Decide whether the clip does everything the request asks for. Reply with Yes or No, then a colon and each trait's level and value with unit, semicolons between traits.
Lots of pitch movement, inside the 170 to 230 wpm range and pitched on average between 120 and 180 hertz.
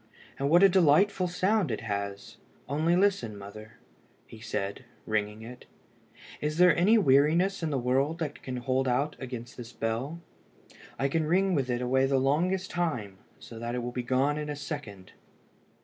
Yes: wide, 5.8 semitones; average, 175 wpm; low, 135 Hz